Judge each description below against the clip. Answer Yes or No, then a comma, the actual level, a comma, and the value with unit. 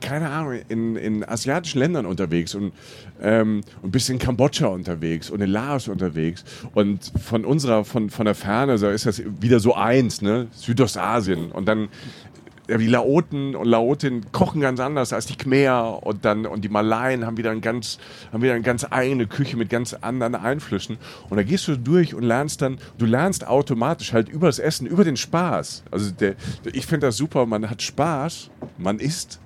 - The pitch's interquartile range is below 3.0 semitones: No, average, 4.1 semitones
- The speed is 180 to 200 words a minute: Yes, average, 185 wpm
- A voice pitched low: Yes, low, 120 Hz